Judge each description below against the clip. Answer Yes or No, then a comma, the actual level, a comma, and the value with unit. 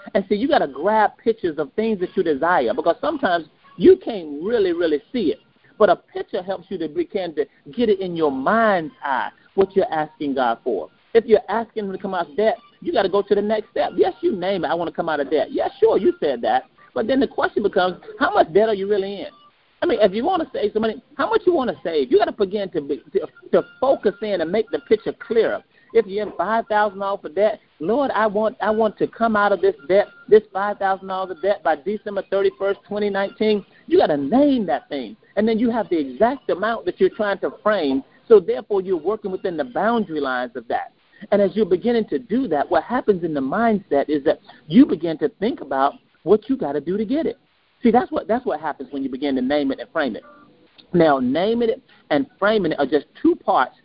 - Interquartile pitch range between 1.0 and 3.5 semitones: No, average, 4.9 semitones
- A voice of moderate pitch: No, high, 210 Hz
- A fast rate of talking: Yes, fast, 240 wpm